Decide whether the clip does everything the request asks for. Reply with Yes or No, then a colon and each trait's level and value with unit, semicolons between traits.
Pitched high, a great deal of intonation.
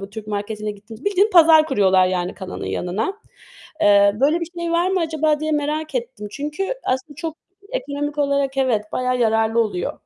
Yes: very high, 270 Hz; wide, 6.7 semitones